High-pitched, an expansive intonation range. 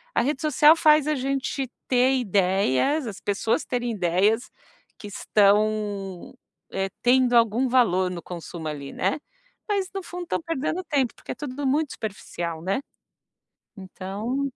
Yes: high, 235 Hz; wide, 6.2 semitones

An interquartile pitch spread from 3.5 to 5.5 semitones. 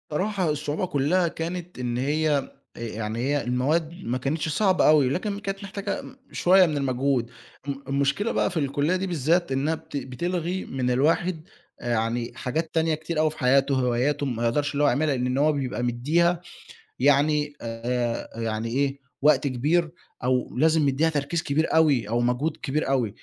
Yes: average, 4.3 semitones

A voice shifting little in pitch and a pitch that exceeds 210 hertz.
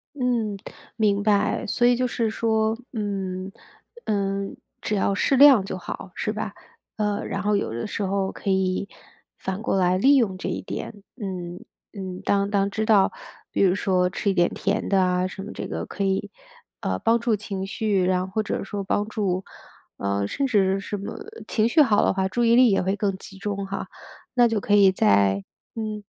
No: narrow, 2.2 semitones; high, 200 Hz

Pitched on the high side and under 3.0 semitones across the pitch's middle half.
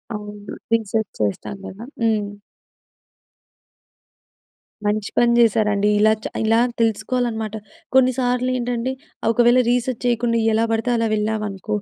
Yes: high, 225 Hz; narrow, 2.4 semitones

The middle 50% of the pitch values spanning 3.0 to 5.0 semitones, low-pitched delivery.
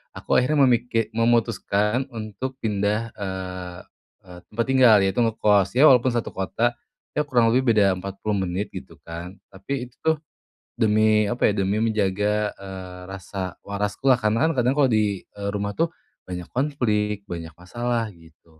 Yes: average, 3.7 semitones; low, 105 Hz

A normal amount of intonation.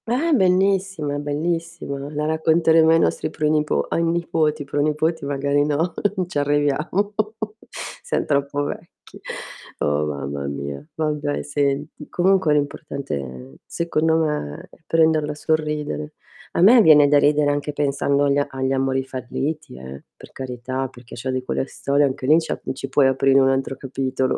Yes: average, 3.0 semitones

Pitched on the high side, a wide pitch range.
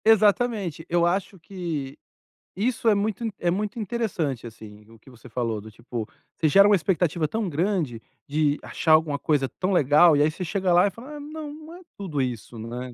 No: medium, 170 Hz; wide, 6.9 semitones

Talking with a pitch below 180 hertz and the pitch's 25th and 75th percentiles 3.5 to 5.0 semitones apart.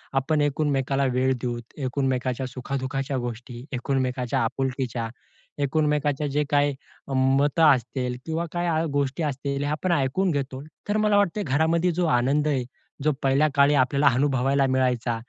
No: low, 135 Hz; narrow, 2.5 semitones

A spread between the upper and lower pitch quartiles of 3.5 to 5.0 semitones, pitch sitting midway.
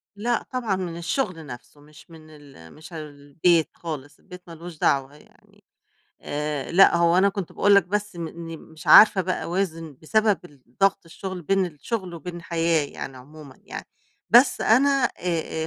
Yes: average, 3.9 semitones; medium, 170 Hz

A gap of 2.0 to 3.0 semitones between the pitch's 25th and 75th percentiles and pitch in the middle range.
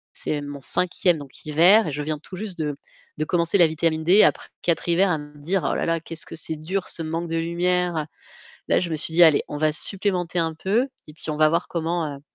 Yes: narrow, 2.4 semitones; medium, 165 Hz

